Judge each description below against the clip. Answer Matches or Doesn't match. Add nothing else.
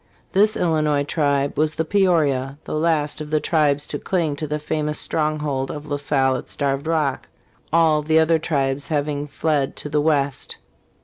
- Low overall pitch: Doesn't match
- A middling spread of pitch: Doesn't match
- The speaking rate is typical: Matches